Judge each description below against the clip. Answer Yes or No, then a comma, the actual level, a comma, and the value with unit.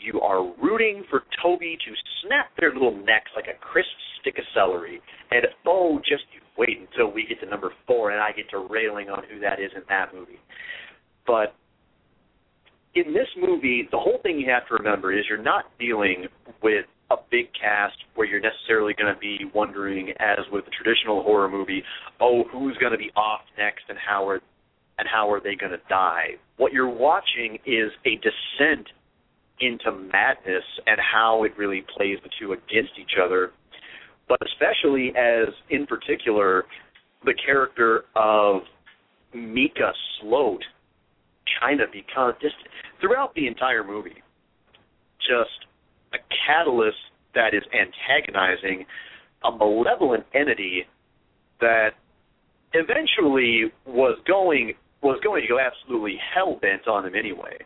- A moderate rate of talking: Yes, average, 150 wpm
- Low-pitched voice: Yes, low, 120 Hz